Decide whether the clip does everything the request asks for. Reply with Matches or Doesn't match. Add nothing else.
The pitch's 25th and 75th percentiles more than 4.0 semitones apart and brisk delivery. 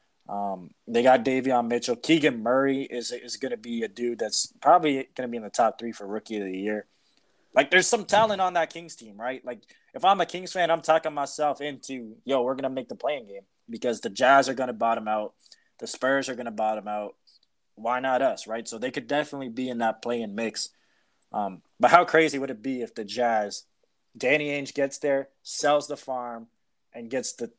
Matches